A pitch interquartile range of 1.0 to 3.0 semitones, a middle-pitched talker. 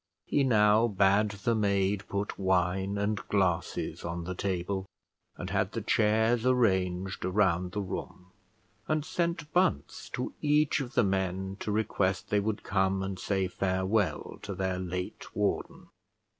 No: narrow, 2.5 semitones; low, 100 Hz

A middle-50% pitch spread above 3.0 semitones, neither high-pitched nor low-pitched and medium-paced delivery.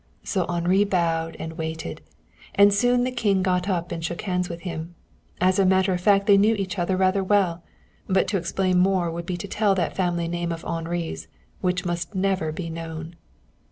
No: narrow, 2.4 semitones; medium, 180 Hz; average, 195 wpm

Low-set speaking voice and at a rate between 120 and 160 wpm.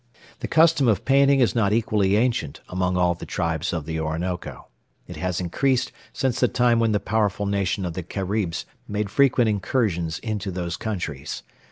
No: low, 100 Hz; average, 175 wpm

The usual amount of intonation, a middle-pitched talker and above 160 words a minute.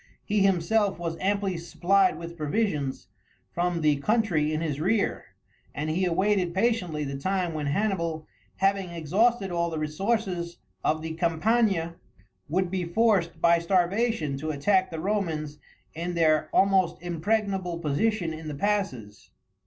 No: average, 3.9 semitones; medium, 175 Hz; average, 140 wpm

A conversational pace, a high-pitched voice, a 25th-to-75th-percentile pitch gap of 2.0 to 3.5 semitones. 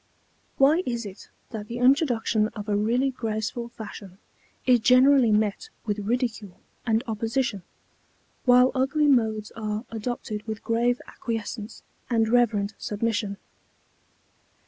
No: slow, 120 wpm; high, 225 Hz; average, 2.7 semitones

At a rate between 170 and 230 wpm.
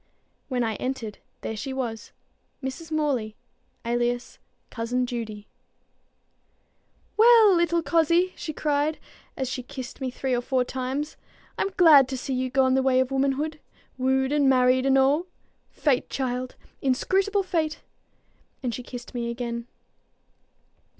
No: slow, 135 wpm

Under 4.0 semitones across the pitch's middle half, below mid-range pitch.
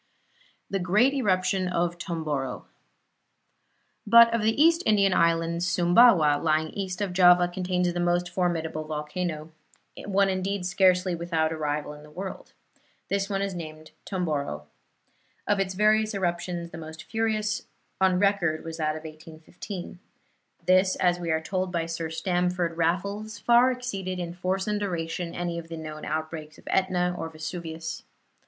No: average, 3.1 semitones; medium, 180 Hz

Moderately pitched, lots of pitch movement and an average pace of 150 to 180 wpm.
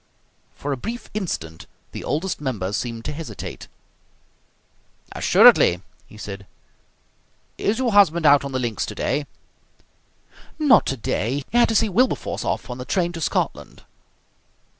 No: medium, 145 Hz; wide, 8.8 semitones; average, 140 wpm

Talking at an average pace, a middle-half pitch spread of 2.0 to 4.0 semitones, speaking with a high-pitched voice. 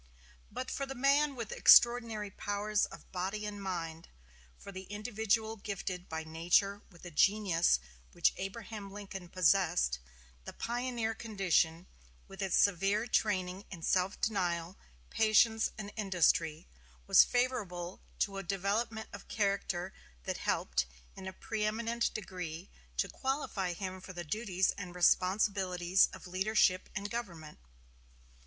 No: slow, 130 wpm; average, 3.3 semitones; high, 195 Hz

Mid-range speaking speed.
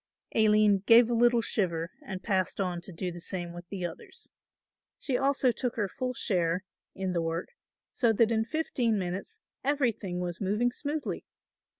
Yes: average, 170 wpm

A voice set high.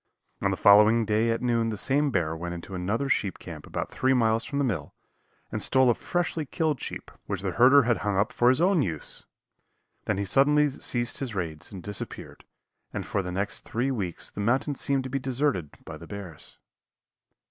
No: low, 115 Hz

